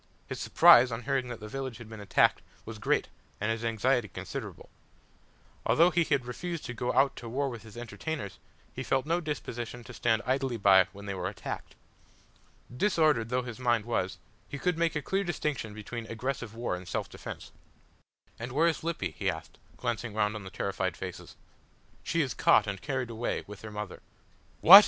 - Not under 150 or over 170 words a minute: No, average, 190 wpm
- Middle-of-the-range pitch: No, low, 120 Hz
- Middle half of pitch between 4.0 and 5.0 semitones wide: Yes, average, 4.3 semitones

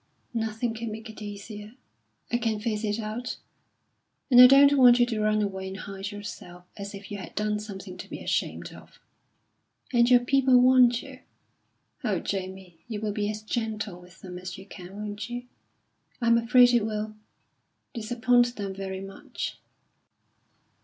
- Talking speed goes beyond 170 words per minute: No, average, 165 wpm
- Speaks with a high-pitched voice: Yes, high, 215 Hz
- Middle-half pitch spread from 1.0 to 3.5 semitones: Yes, average, 3.2 semitones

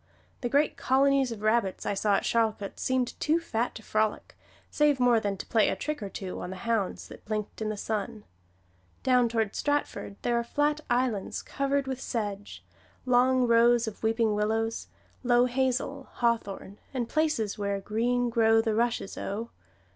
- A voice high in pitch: Yes, high, 230 Hz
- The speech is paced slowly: No, average, 175 wpm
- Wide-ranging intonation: No, average, 3.0 semitones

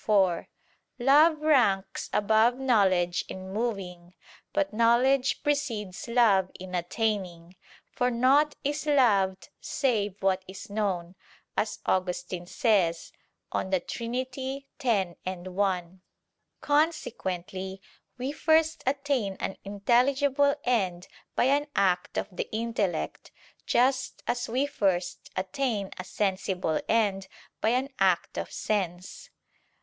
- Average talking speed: No, slow, 110 wpm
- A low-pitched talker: No, high, 210 Hz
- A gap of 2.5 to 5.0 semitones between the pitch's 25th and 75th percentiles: No, wide, 5.6 semitones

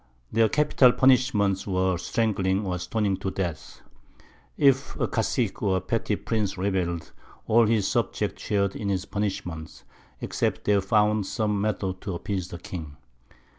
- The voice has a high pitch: No, low, 100 Hz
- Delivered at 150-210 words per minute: No, average, 140 wpm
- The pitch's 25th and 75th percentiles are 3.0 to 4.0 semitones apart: No, narrow, 2.6 semitones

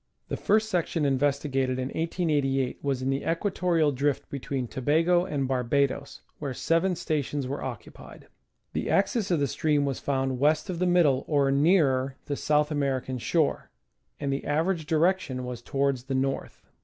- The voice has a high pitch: No, medium, 140 Hz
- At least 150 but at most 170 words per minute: Yes, average, 160 wpm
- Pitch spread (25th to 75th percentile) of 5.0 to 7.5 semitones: No, average, 3.6 semitones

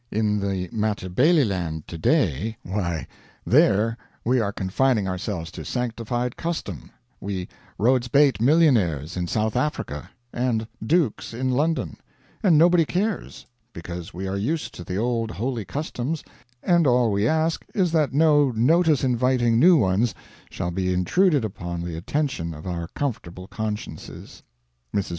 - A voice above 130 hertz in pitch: No, low, 115 Hz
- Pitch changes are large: Yes, wide, 7.2 semitones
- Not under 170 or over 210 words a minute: No, average, 140 wpm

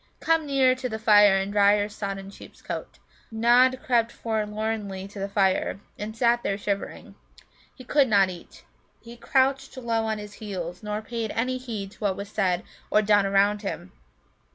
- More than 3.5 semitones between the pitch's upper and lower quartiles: No, average, 3.0 semitones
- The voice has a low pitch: No, high, 210 Hz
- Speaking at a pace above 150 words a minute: Yes, average, 175 wpm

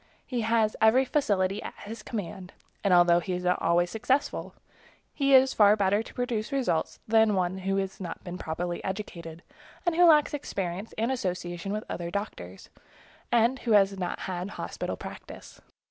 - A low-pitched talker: No, high, 200 Hz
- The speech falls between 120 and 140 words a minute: No, average, 175 wpm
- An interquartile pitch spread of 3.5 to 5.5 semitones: Yes, average, 4.2 semitones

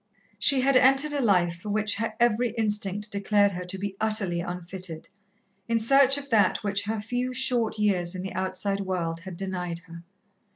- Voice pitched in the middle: No, high, 205 Hz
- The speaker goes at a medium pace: Yes, average, 180 wpm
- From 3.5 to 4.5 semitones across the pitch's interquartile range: Yes, average, 3.9 semitones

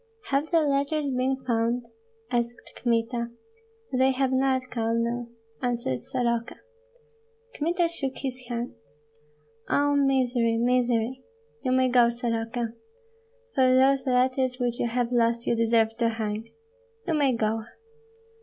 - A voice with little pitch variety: Yes, narrow, 2.1 semitones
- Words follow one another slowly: Yes, slow, 125 wpm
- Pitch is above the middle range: Yes, high, 245 Hz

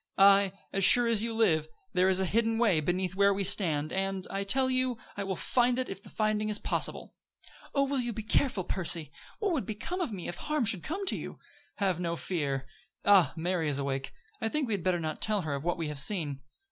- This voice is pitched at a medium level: No, high, 195 Hz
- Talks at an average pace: No, fast, 235 wpm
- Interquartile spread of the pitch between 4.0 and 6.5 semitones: Yes, average, 4.8 semitones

